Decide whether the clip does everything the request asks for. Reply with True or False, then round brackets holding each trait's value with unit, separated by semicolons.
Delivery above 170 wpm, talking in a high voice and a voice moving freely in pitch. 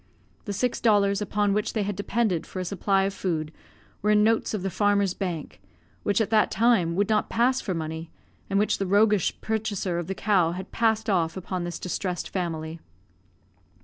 False (190 wpm; 200 Hz; 2.9 semitones)